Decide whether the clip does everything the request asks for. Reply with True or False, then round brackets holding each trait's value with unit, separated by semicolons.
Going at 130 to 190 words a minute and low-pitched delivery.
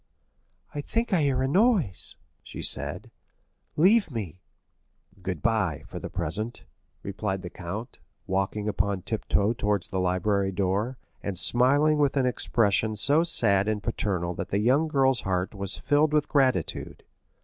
True (150 wpm; 110 Hz)